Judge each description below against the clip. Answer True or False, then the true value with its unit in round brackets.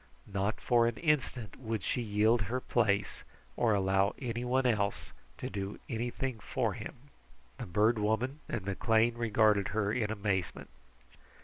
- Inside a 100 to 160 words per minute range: True (140 wpm)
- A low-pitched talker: True (110 Hz)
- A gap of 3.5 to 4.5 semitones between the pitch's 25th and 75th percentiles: False (2.9 semitones)